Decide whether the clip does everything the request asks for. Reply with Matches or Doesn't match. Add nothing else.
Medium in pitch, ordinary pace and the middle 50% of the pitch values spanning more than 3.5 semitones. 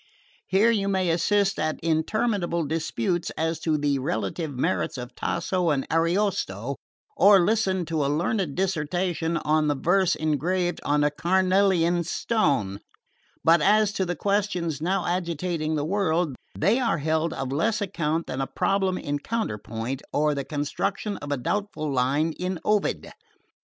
Matches